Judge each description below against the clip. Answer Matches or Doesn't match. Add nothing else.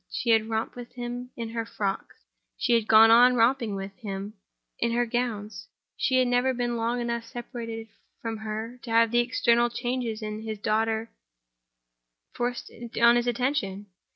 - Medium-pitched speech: Doesn't match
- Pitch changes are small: Matches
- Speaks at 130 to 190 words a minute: Matches